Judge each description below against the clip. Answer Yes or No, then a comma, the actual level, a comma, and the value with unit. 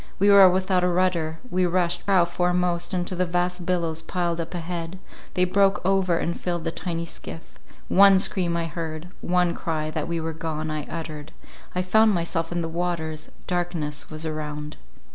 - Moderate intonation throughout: No, narrow, 2.0 semitones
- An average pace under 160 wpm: No, average, 175 wpm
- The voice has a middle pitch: Yes, medium, 175 Hz